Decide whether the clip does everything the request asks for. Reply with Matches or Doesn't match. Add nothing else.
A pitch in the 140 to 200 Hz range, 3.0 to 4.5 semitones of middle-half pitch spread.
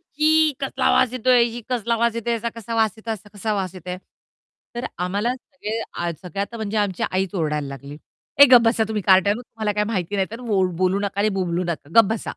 Doesn't match